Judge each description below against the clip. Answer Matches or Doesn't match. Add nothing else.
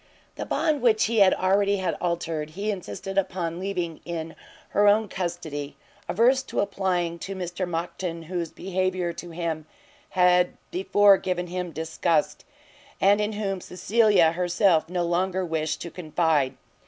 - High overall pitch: Doesn't match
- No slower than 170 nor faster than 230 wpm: Doesn't match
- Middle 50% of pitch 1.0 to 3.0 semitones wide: Matches